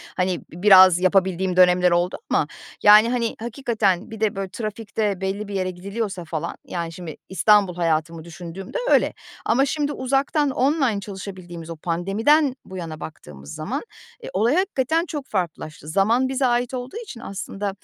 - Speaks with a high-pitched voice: Yes, high, 195 Hz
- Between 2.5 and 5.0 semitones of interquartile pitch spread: No, wide, 5.4 semitones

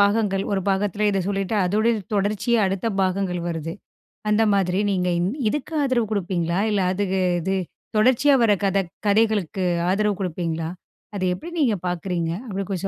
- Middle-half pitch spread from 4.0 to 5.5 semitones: No, narrow, 2.6 semitones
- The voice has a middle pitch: No, high, 195 Hz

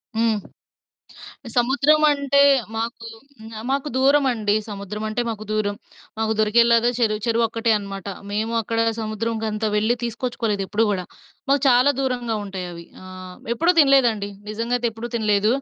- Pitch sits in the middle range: No, high, 225 Hz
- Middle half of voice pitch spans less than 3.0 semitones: Yes, narrow, 2.4 semitones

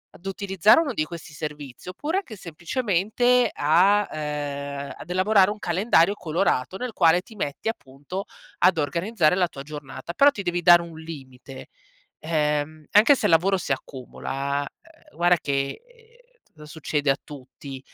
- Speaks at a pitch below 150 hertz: No, medium, 170 Hz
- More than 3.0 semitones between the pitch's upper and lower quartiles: Yes, average, 5.1 semitones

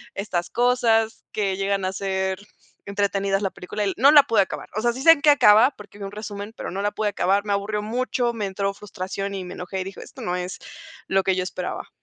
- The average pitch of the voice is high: Yes, high, 200 Hz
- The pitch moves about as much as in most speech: No, narrow, 2.3 semitones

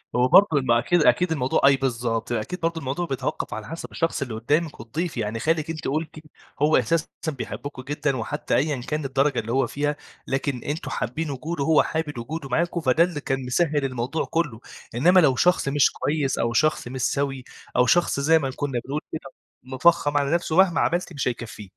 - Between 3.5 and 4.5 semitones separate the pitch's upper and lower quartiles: Yes, average, 4.1 semitones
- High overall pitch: No, medium, 140 Hz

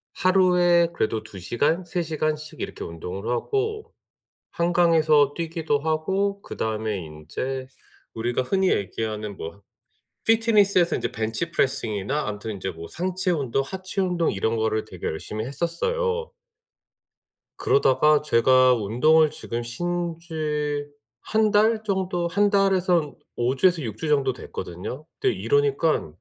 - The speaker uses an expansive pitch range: Yes, wide, 7.7 semitones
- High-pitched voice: No, medium, 150 Hz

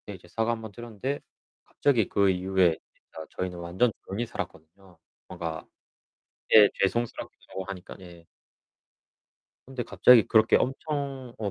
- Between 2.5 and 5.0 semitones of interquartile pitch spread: Yes, average, 4.6 semitones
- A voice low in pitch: Yes, low, 100 Hz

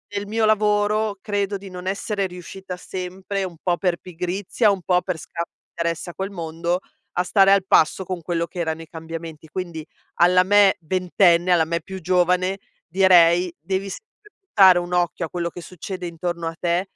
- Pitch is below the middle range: No, medium, 180 Hz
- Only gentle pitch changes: Yes, narrow, 2.1 semitones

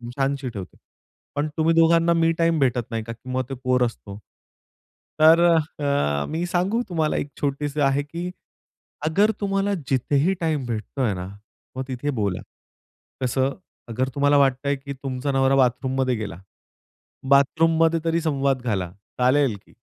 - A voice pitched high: No, medium, 140 Hz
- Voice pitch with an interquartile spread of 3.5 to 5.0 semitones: Yes, average, 4.2 semitones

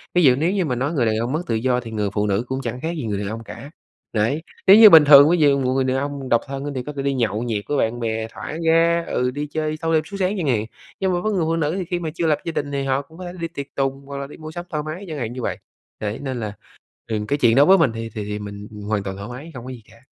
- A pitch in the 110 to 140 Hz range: Yes, low, 135 Hz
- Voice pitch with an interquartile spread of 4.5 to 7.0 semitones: Yes, wide, 5.5 semitones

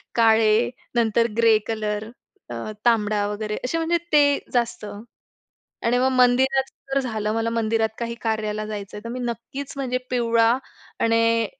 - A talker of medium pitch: No, high, 230 Hz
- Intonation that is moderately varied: No, narrow, 2.3 semitones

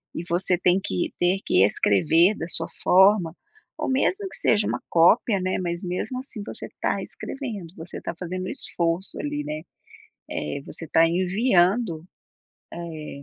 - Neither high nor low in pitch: Yes, medium, 180 Hz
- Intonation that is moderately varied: Yes, average, 3.2 semitones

